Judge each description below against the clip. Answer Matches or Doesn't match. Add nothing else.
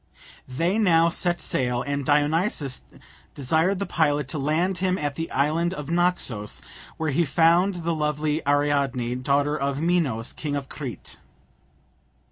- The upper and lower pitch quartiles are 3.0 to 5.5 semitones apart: Matches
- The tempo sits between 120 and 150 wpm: Matches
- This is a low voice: Doesn't match